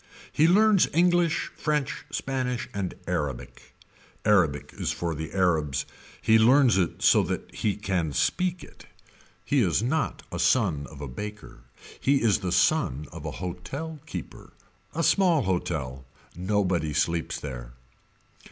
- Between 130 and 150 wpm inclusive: Yes, average, 140 wpm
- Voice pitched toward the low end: Yes, low, 100 Hz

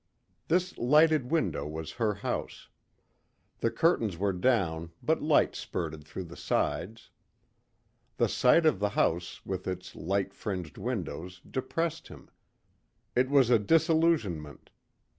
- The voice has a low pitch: Yes, low, 105 Hz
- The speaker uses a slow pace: Yes, slow, 125 wpm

